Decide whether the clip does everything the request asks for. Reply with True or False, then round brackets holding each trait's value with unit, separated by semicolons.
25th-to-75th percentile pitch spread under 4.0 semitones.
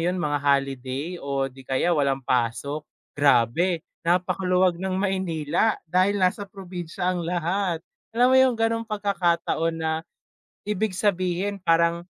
False (4.3 semitones)